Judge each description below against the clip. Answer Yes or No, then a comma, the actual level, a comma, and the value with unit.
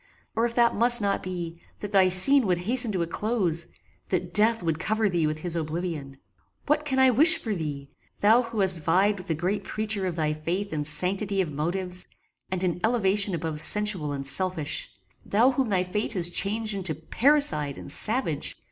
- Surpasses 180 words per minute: Yes, average, 190 wpm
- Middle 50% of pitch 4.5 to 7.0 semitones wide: Yes, average, 4.8 semitones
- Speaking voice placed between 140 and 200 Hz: Yes, high, 190 Hz